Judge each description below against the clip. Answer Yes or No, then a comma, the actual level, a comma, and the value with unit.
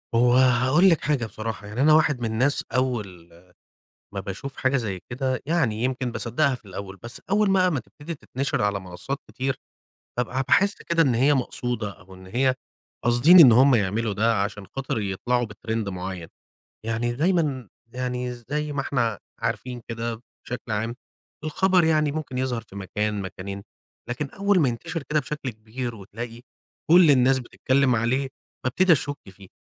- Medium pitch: No, low, 125 Hz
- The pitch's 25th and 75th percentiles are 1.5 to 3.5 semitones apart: No, average, 4.3 semitones